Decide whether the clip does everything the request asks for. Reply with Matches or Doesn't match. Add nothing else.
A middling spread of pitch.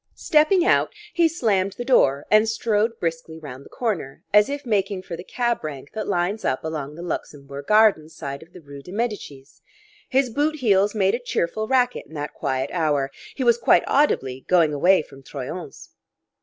Doesn't match